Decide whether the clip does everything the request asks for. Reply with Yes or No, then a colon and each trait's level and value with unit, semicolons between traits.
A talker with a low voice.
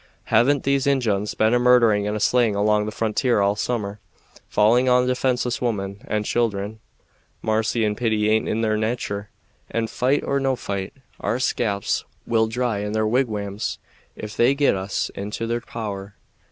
Yes: low, 110 Hz